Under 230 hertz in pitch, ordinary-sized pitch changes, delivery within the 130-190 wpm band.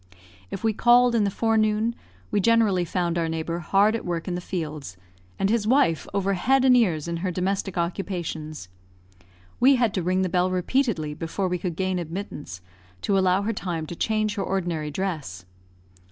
Yes: medium, 185 Hz; average, 4.0 semitones; average, 180 wpm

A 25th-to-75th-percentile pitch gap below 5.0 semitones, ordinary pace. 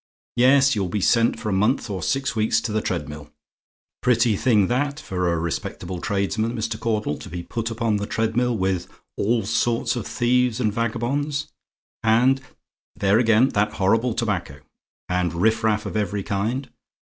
Yes: average, 3.5 semitones; average, 160 wpm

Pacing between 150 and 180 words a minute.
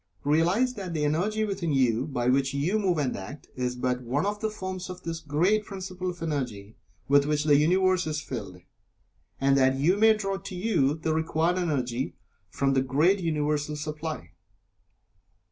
Yes: average, 175 wpm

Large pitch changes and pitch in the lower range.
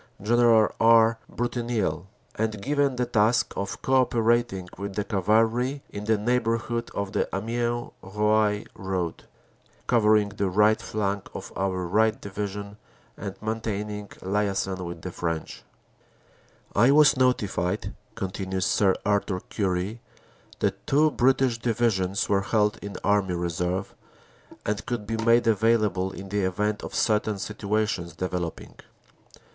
No: average, 3.0 semitones; low, 105 Hz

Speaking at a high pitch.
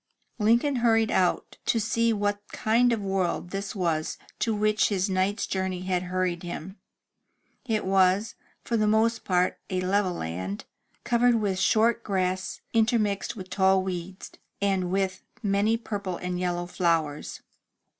Yes: high, 195 Hz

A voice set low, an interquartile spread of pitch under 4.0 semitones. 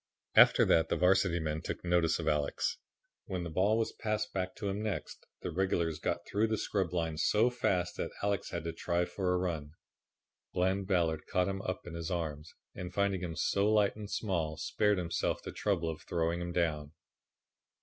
Yes: very low, 90 Hz; average, 3.1 semitones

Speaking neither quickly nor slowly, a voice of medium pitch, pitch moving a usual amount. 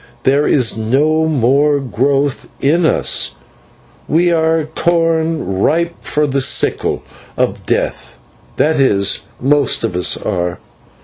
No: slow, 120 wpm; medium, 145 Hz; average, 3.9 semitones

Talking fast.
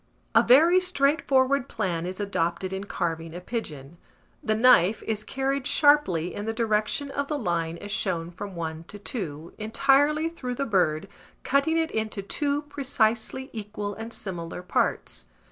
No: average, 155 wpm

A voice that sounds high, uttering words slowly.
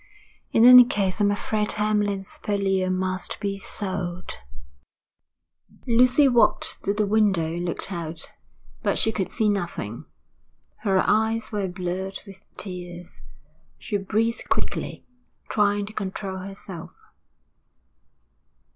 Yes: high, 200 Hz; slow, 115 wpm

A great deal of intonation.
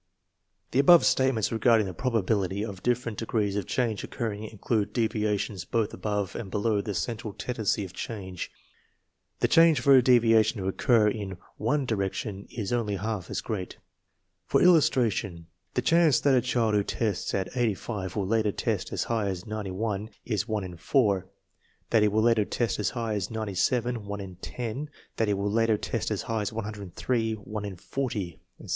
No: average, 2.7 semitones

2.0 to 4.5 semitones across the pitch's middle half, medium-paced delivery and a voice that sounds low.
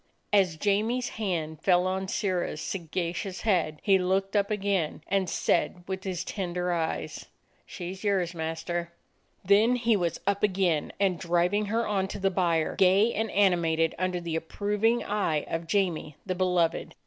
No: average, 2.8 semitones; average, 160 wpm; medium, 185 Hz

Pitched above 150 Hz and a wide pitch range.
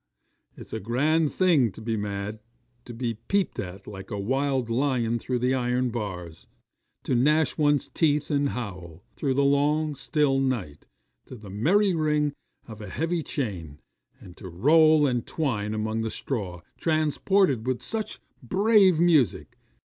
No: low, 130 Hz; wide, 5.9 semitones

